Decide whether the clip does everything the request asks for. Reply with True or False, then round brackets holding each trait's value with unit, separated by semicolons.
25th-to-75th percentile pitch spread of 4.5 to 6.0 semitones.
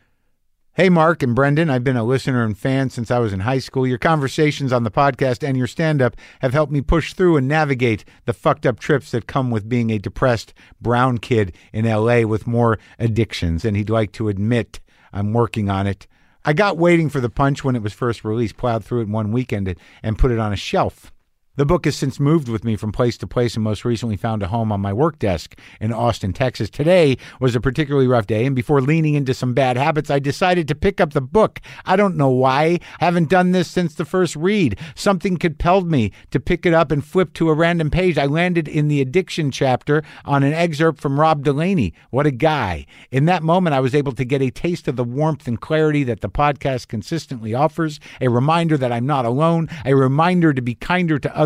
True (5.2 semitones)